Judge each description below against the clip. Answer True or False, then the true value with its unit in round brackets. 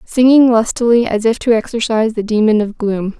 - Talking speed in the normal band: True (190 wpm)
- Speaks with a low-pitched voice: False (225 Hz)